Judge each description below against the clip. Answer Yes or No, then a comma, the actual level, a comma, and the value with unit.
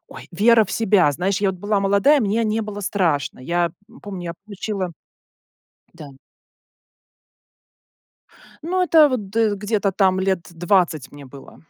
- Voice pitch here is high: Yes, high, 195 Hz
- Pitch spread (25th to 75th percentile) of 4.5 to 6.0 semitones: No, average, 3.6 semitones